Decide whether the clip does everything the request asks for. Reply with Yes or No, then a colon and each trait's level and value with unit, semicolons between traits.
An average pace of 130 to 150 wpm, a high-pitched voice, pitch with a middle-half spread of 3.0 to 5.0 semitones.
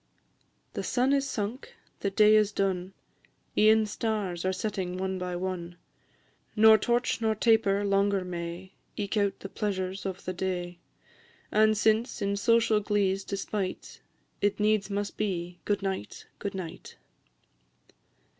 No: slow, 135 wpm; high, 200 Hz; narrow, 2.4 semitones